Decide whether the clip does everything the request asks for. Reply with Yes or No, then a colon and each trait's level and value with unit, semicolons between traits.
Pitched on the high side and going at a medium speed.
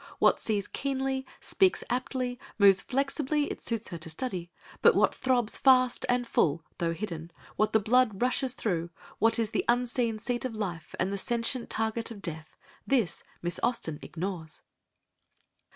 Yes: high, 225 Hz; average, 160 wpm